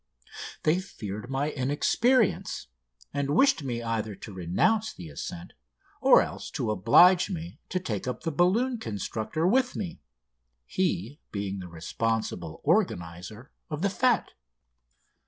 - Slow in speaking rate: Yes, slow, 130 wpm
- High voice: No, low, 135 Hz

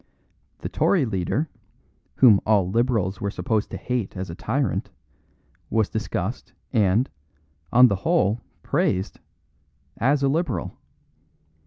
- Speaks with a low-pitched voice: Yes, low, 110 Hz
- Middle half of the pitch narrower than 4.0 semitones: No, average, 4.7 semitones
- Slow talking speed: Yes, slow, 120 wpm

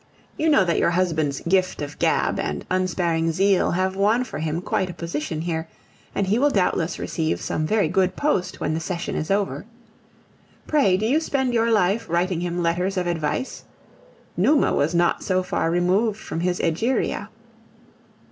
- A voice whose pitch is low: No, medium, 180 Hz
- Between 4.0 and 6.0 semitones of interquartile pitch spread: No, average, 3.3 semitones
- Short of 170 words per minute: No, average, 175 wpm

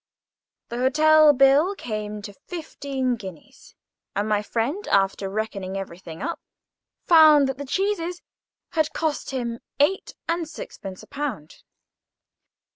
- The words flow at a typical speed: No, slow, 120 wpm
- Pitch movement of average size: No, wide, 6.9 semitones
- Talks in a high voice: Yes, very high, 270 Hz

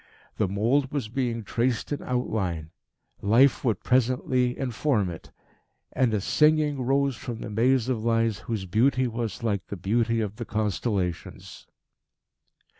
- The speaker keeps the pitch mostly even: No, average, 3.5 semitones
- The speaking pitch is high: No, low, 115 Hz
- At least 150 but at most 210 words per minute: No, average, 140 wpm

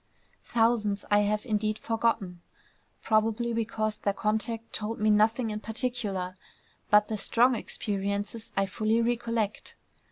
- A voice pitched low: No, high, 215 Hz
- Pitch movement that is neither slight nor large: No, narrow, 1.7 semitones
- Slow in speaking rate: Yes, slow, 125 wpm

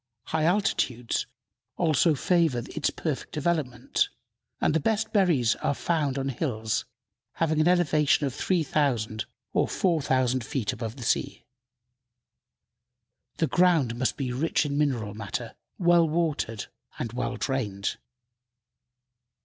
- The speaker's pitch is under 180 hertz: Yes, medium, 140 Hz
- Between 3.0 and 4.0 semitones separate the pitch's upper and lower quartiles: No, average, 5.1 semitones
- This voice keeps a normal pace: No, slow, 120 wpm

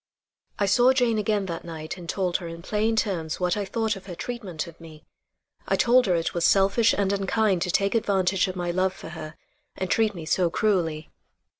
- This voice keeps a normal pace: No, fast, 210 wpm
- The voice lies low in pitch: No, high, 190 Hz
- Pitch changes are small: No, average, 3.7 semitones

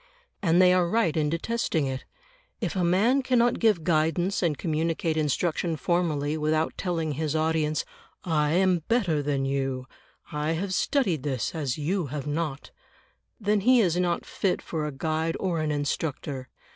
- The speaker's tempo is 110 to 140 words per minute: No, average, 160 wpm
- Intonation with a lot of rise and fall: No, average, 3.4 semitones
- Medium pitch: Yes, medium, 160 Hz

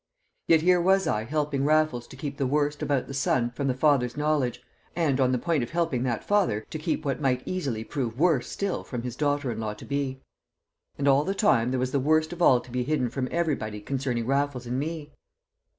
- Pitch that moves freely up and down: No, average, 3.7 semitones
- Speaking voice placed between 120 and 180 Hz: Yes, medium, 140 Hz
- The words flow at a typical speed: No, fast, 225 wpm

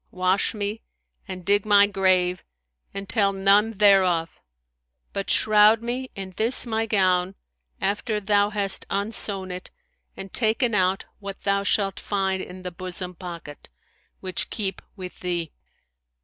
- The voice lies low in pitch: No, high, 195 Hz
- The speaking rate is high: No, slow, 135 wpm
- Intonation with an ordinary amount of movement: No, narrow, 2.2 semitones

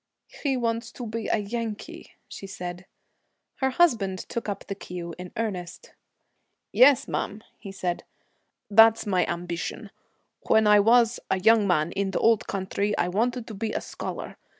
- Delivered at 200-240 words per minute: No, average, 160 wpm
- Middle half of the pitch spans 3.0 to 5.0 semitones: Yes, average, 3.5 semitones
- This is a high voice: Yes, high, 210 Hz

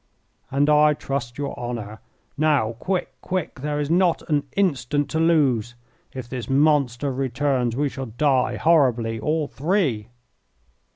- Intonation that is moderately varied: Yes, average, 3.7 semitones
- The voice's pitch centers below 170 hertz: Yes, medium, 140 Hz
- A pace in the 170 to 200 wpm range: No, slow, 135 wpm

